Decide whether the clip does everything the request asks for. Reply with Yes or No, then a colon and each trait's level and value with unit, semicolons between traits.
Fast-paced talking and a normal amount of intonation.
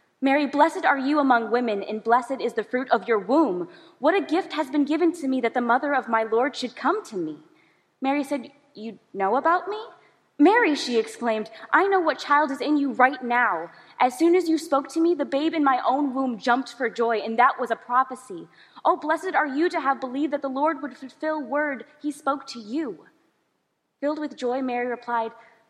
Yes: fast, 215 wpm; average, 4.4 semitones